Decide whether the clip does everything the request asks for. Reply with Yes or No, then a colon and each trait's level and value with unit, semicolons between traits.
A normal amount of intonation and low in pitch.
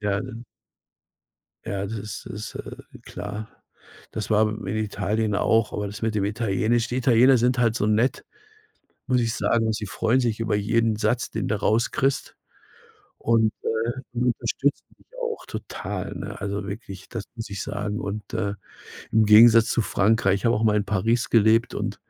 No: narrow, 1.9 semitones; low, 110 Hz